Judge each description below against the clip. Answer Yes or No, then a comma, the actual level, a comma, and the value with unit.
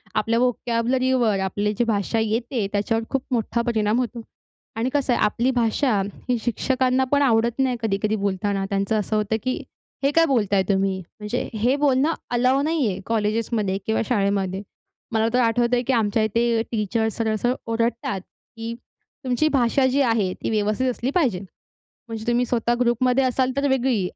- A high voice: Yes, high, 230 Hz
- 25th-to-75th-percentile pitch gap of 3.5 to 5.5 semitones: No, average, 3.1 semitones